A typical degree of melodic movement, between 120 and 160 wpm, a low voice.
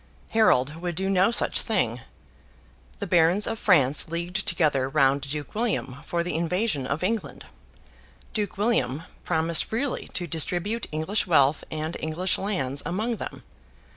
No: average, 5.0 semitones; average, 140 wpm; medium, 170 Hz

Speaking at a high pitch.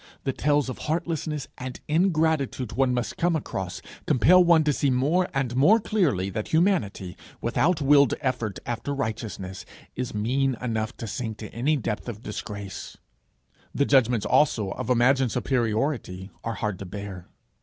No: low, 125 Hz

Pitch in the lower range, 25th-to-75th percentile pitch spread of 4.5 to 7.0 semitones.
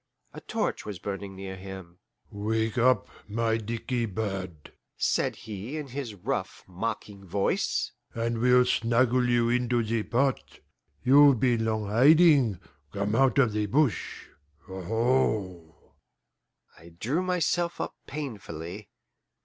No: low, 115 Hz; average, 4.1 semitones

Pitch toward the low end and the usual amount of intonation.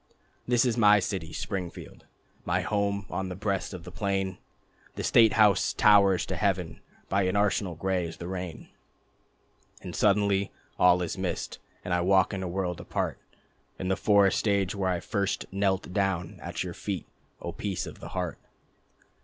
No: very low, 95 Hz; narrow, 1.9 semitones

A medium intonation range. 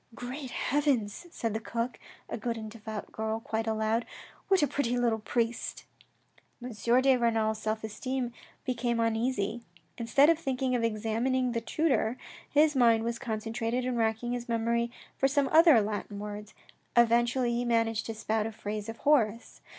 No: narrow, 2.2 semitones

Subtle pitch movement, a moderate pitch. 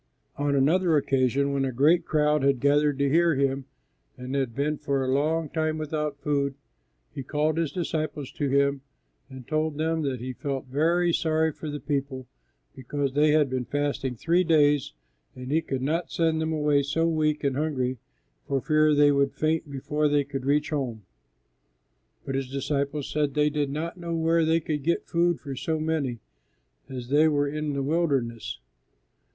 Yes: narrow, 2.3 semitones; medium, 145 Hz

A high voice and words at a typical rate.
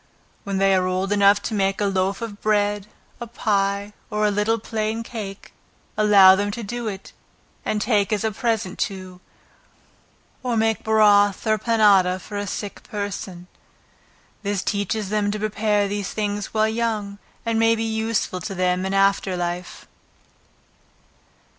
Yes: high, 205 Hz; average, 155 wpm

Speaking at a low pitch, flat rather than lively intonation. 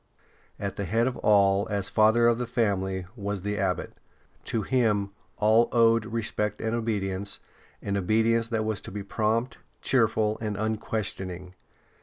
Yes: low, 110 Hz; narrow, 2.3 semitones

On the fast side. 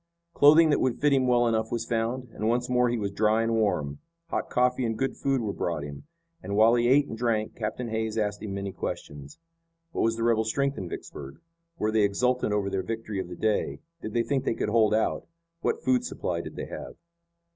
Yes: fast, 225 wpm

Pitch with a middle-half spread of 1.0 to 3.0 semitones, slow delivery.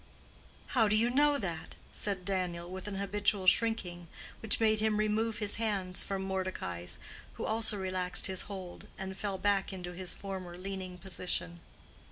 No: narrow, 2.5 semitones; average, 160 wpm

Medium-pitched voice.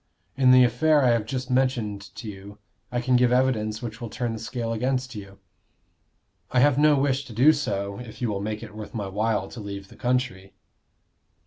No: low, 120 Hz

